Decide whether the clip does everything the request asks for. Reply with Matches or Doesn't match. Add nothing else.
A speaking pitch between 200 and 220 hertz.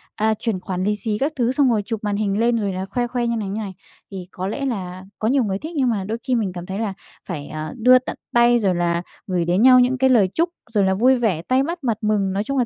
Matches